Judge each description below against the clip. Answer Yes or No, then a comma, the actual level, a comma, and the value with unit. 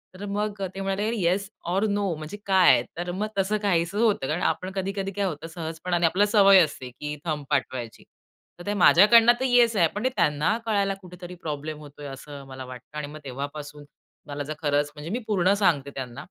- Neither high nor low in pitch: Yes, medium, 175 Hz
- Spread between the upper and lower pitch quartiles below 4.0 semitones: No, average, 5.2 semitones